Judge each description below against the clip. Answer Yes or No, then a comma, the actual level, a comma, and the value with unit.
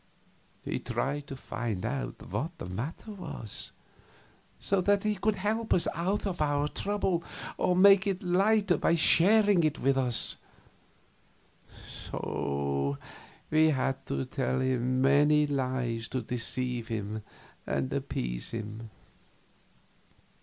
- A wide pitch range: Yes, wide, 7.5 semitones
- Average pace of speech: No, slow, 120 wpm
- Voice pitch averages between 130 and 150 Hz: Yes, medium, 140 Hz